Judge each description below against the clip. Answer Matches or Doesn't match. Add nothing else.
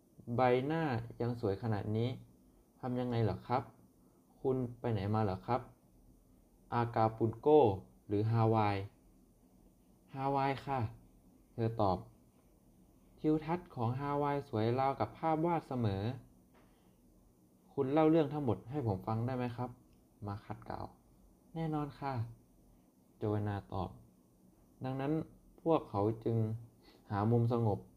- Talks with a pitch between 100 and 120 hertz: Matches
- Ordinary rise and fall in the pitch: Doesn't match